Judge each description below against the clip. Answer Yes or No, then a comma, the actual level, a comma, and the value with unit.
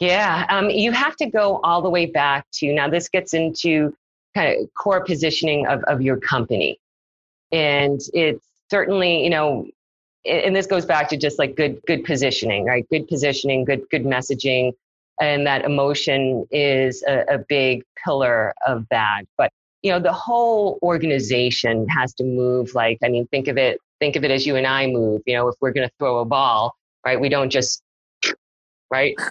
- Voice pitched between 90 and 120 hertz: No, medium, 140 Hz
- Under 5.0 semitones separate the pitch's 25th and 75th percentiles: Yes, average, 4.4 semitones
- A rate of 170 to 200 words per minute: Yes, average, 185 wpm